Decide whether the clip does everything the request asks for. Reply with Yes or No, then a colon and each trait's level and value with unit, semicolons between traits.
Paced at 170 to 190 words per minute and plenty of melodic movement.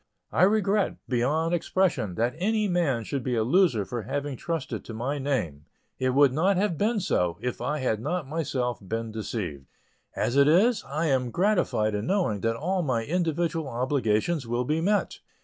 Yes: average, 180 wpm; wide, 6.8 semitones